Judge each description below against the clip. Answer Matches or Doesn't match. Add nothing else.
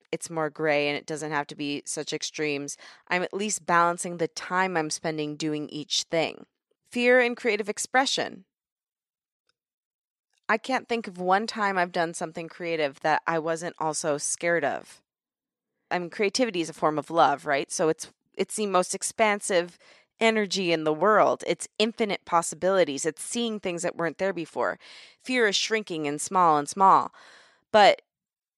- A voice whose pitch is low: Doesn't match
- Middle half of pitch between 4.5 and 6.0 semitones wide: Matches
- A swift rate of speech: Doesn't match